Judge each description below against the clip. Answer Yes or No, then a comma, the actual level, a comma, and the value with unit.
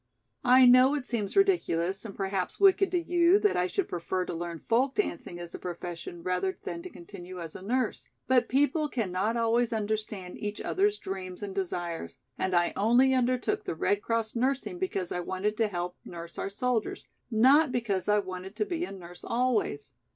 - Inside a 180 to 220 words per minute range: Yes, average, 190 wpm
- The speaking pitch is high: Yes, high, 210 Hz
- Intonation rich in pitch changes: Yes, wide, 5.9 semitones